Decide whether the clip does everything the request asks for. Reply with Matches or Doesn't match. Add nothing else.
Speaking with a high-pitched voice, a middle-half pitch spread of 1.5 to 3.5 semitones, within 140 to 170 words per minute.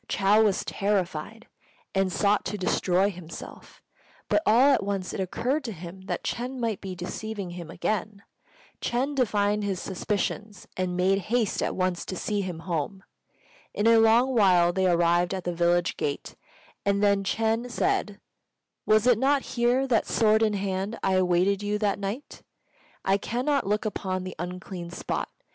Matches